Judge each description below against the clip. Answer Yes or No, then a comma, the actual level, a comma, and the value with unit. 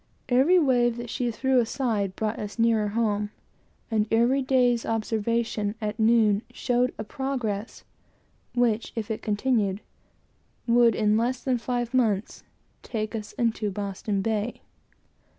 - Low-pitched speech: No, high, 225 Hz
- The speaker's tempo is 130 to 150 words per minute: Yes, slow, 135 wpm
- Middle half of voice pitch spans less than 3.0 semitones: Yes, narrow, 2.5 semitones